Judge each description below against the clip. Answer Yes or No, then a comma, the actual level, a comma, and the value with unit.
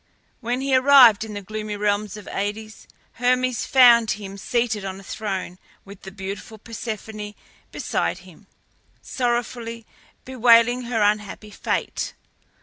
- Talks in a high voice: Yes, high, 220 Hz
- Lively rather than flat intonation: No, average, 2.8 semitones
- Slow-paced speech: Yes, slow, 130 wpm